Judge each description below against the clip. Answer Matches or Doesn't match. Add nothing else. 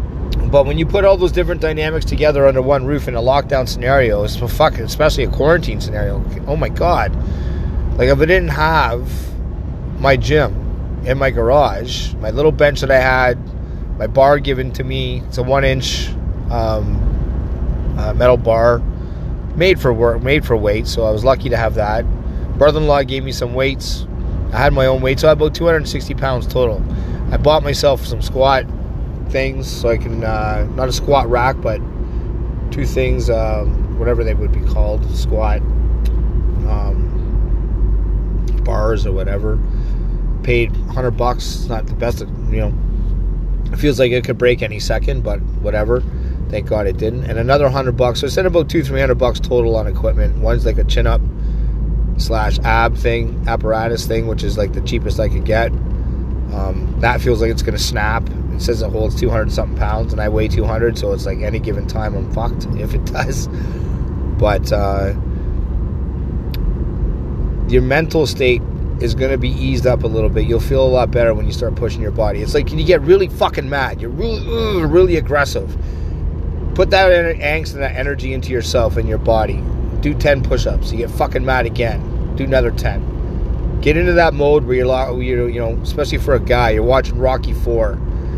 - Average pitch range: Doesn't match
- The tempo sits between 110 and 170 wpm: Doesn't match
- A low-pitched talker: Matches